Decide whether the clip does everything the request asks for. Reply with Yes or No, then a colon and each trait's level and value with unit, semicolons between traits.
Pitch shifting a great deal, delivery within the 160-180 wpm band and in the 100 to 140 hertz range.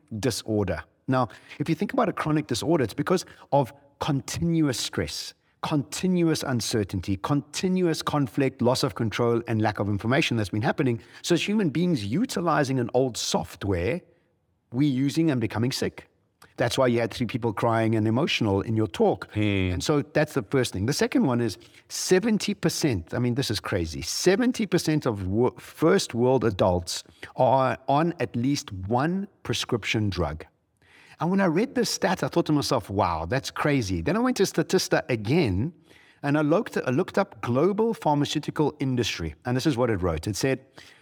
Yes: wide, 6.4 semitones; average, 170 wpm; low, 135 Hz